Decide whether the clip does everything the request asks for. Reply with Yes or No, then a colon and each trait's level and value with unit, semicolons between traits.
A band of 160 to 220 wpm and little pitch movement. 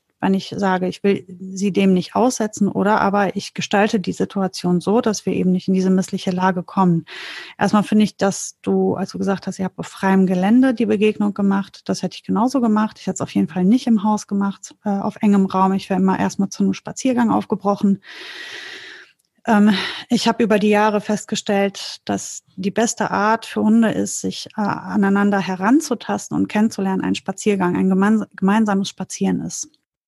Yes: average, 185 wpm; narrow, 2.2 semitones